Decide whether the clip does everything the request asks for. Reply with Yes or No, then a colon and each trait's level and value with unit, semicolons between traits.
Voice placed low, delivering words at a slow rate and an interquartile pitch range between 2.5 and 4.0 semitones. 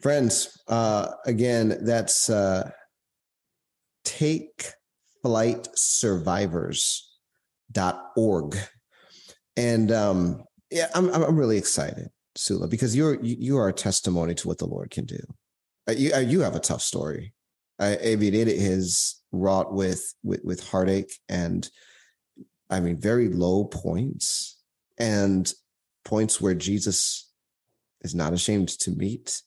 Yes: low, 105 Hz; slow, 115 wpm; average, 3.7 semitones